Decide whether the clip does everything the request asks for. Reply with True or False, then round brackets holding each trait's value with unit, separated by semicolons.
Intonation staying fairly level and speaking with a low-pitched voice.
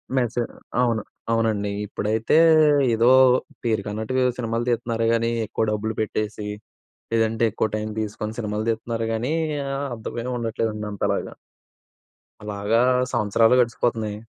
True (1.6 semitones; 115 Hz)